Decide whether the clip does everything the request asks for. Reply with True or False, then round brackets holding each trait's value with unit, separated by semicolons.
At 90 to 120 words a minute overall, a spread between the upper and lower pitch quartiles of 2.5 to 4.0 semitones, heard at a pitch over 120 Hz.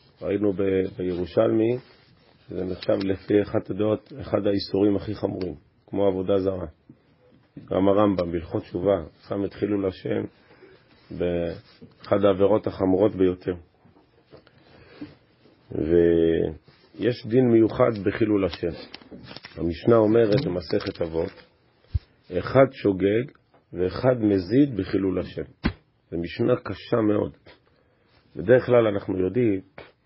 False (100 wpm; 2.8 semitones; 100 Hz)